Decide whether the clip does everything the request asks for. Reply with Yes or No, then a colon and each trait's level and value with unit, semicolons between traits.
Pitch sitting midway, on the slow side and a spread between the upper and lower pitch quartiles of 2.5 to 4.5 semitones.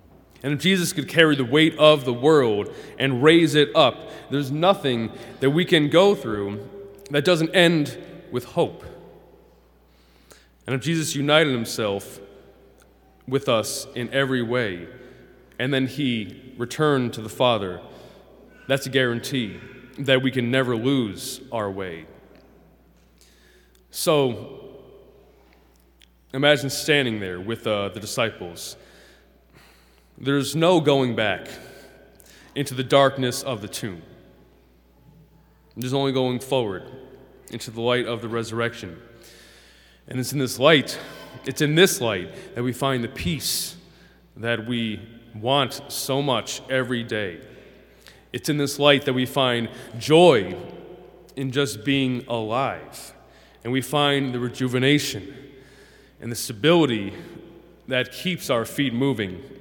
No: low, 130 Hz; slow, 130 wpm; average, 3.5 semitones